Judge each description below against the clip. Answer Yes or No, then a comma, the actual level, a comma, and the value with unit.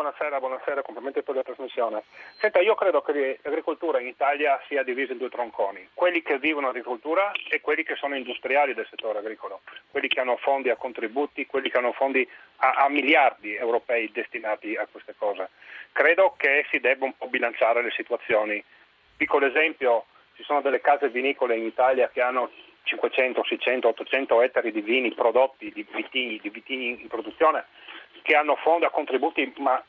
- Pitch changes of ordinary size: Yes, average, 3.1 semitones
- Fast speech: Yes, fast, 175 wpm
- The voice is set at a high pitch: No, low, 135 Hz